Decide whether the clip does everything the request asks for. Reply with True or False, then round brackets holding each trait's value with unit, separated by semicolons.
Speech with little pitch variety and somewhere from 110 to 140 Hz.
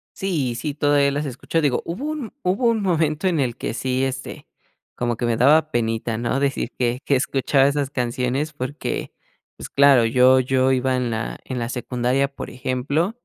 False (3.2 semitones; 135 Hz)